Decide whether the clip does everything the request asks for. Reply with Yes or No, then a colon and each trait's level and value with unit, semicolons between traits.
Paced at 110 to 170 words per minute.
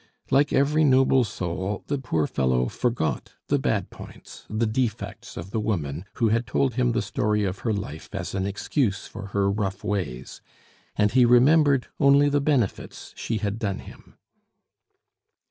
Yes: average, 165 wpm